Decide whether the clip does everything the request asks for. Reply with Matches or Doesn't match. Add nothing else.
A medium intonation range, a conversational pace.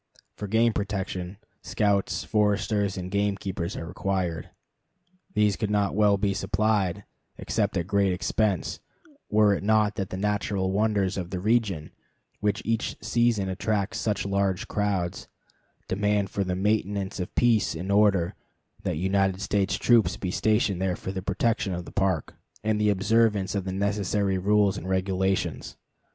Doesn't match